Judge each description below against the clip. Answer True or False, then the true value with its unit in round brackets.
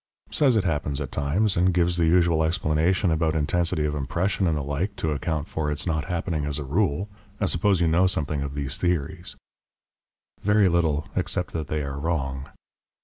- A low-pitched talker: True (80 Hz)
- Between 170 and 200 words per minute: True (195 wpm)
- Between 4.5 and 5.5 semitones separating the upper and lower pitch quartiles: False (3.4 semitones)